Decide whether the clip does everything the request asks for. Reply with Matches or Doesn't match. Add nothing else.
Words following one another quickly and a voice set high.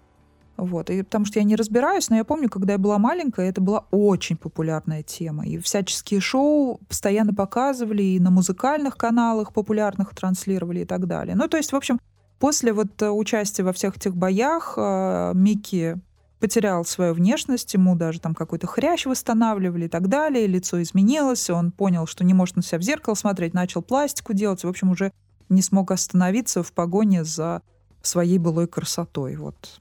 Matches